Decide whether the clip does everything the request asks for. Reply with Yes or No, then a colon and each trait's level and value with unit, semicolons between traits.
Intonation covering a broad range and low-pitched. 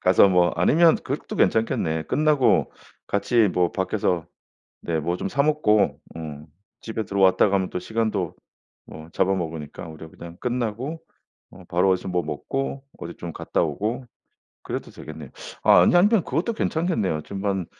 Yes: wide, 6.0 semitones; very low, 95 Hz